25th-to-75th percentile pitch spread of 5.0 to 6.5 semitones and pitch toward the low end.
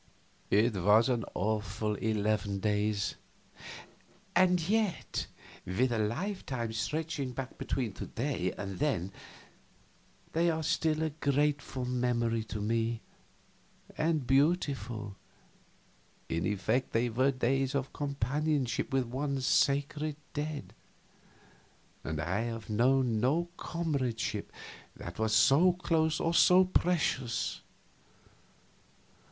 Yes: wide, 5.4 semitones; low, 125 Hz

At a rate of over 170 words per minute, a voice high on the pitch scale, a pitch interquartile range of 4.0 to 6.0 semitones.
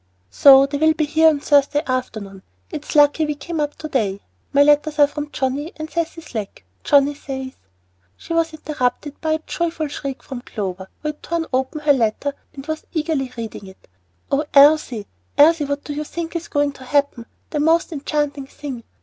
No: average, 190 wpm; very high, 290 Hz; average, 2.8 semitones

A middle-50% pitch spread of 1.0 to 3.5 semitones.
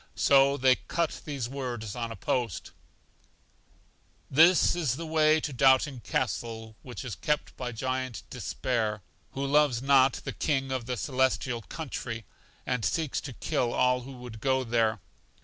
Yes: average, 2.8 semitones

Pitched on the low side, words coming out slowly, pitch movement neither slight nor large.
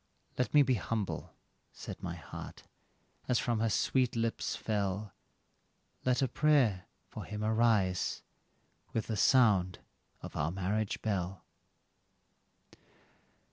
Yes: low, 110 Hz; slow, 115 wpm; average, 3.7 semitones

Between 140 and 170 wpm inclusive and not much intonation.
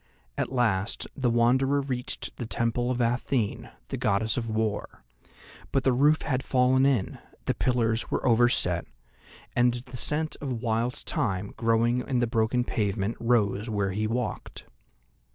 Yes: average, 150 wpm; narrow, 2.2 semitones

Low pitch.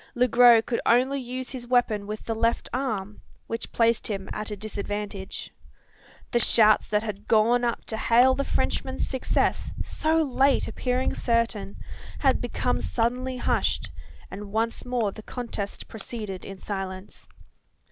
No: high, 230 Hz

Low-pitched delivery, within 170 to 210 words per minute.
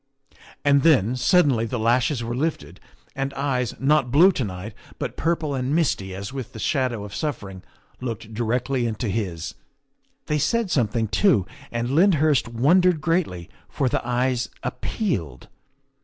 No: low, 125 Hz; average, 145 wpm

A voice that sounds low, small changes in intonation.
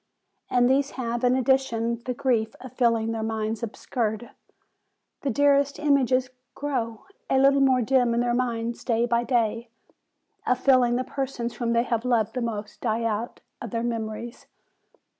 No: high, 240 Hz; narrow, 2.1 semitones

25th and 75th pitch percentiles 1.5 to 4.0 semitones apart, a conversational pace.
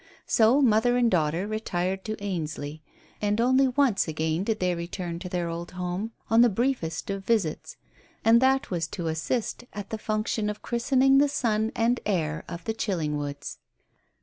No: wide, 5.4 semitones; average, 170 wpm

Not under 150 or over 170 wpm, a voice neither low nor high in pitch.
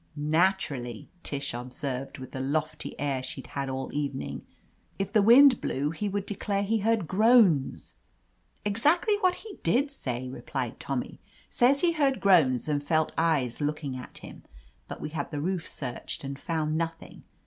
Yes: average, 160 wpm; medium, 155 Hz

